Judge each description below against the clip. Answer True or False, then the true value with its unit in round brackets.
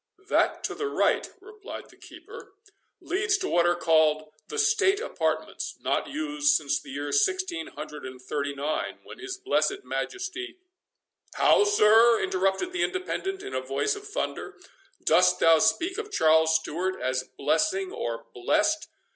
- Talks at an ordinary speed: True (155 wpm)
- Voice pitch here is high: True (235 Hz)